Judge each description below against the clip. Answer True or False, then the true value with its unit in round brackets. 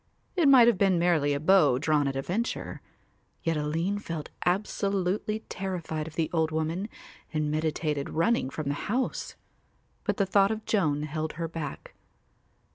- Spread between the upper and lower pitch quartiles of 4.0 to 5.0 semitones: True (4.4 semitones)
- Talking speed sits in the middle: True (160 wpm)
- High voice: False (165 Hz)